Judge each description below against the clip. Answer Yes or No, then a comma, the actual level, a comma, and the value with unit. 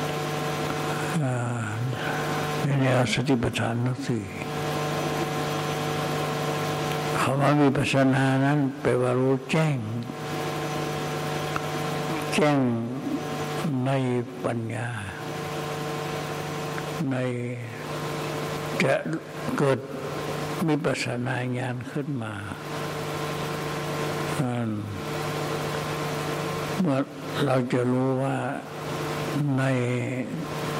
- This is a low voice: No, medium, 150 Hz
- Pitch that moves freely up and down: No, narrow, 2.6 semitones